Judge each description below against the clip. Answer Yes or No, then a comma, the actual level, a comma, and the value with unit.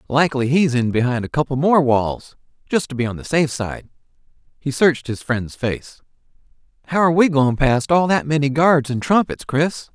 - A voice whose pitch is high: No, medium, 140 Hz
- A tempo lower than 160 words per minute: No, average, 195 wpm